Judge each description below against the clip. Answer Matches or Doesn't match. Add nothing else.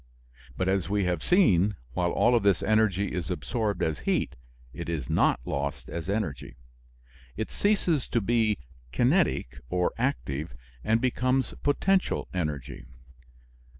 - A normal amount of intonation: Doesn't match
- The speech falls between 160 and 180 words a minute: Doesn't match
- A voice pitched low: Matches